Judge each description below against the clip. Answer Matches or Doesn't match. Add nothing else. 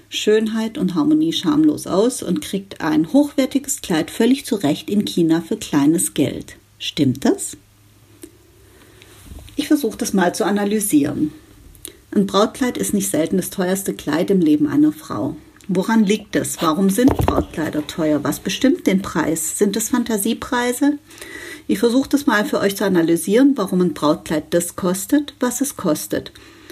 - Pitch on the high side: Matches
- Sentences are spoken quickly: Doesn't match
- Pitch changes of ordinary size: Doesn't match